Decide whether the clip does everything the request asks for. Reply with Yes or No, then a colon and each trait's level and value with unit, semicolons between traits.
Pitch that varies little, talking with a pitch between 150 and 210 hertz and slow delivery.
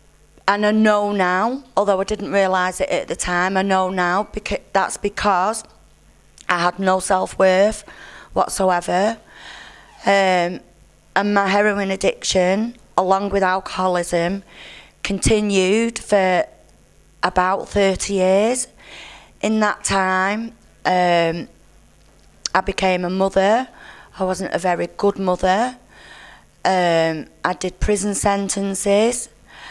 Yes: narrow, 1.9 semitones; high, 190 Hz; slow, 110 wpm